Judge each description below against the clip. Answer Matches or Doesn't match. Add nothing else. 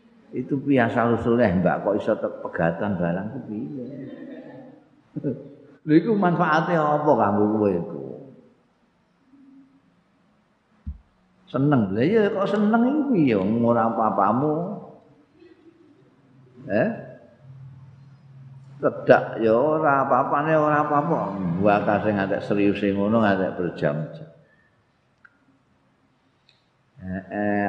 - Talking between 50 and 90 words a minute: Matches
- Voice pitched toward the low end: Matches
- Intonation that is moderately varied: Doesn't match